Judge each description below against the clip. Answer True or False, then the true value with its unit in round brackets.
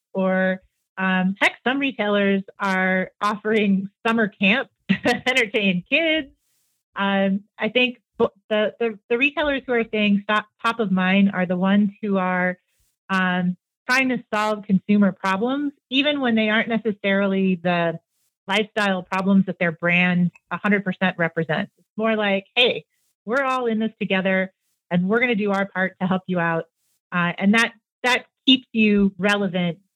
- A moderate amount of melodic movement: True (3.5 semitones)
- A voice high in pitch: True (200 Hz)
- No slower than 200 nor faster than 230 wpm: False (155 wpm)